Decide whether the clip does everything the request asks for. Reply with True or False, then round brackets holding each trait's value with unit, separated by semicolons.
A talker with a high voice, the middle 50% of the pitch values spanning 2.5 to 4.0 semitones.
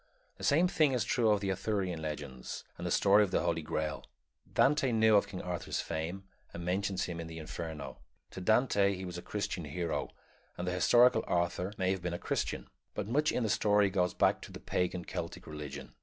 False (90 Hz; 3.6 semitones)